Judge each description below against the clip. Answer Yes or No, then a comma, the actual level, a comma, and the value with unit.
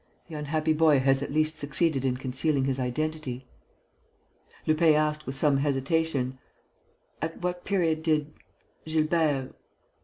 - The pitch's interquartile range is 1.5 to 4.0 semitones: Yes, average, 2.8 semitones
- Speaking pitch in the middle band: Yes, medium, 150 Hz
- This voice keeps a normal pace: No, slow, 125 wpm